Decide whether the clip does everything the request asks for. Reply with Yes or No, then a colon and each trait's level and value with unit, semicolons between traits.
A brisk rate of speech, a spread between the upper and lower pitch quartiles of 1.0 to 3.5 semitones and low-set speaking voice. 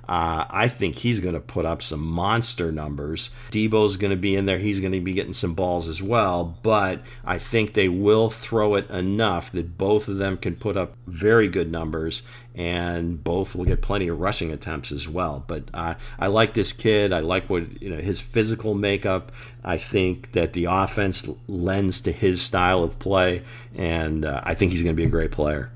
No: fast, 210 wpm; average, 3.9 semitones; very low, 95 Hz